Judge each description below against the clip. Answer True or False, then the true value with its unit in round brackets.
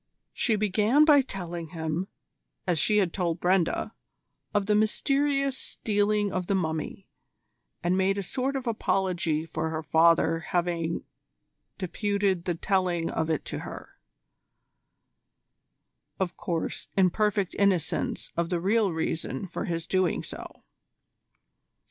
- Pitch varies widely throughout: False (3.7 semitones)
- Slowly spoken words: True (130 wpm)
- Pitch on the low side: False (185 Hz)